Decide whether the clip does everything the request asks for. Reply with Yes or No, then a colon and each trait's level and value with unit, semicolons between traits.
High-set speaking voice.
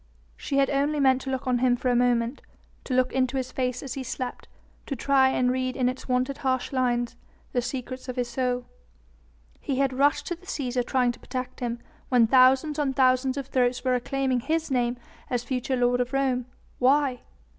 Yes: very high, 255 Hz